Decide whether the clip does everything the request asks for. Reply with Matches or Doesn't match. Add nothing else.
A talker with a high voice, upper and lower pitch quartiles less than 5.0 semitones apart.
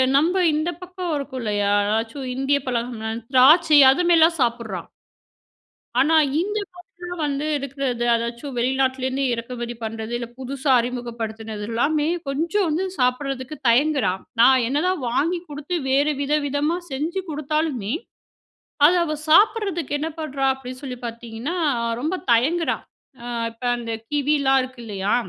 Matches